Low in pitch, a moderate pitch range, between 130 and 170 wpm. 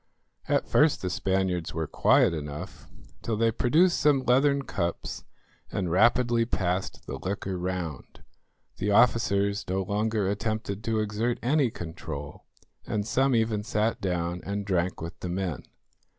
Yes: low, 100 Hz; average, 4.3 semitones; average, 140 wpm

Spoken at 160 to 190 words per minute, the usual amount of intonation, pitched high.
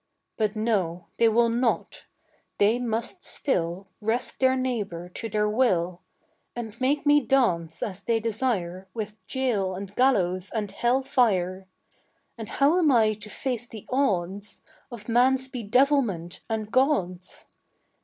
No: slow, 135 wpm; average, 4.8 semitones; high, 220 Hz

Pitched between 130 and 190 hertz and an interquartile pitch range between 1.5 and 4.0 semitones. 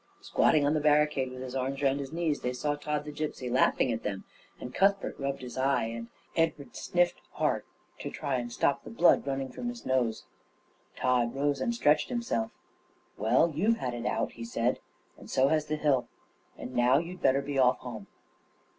Yes: low, 135 Hz; average, 3.3 semitones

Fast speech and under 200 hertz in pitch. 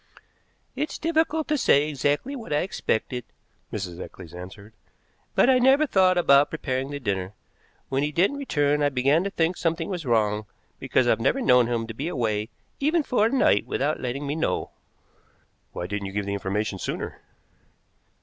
No: average, 170 wpm; medium, 140 Hz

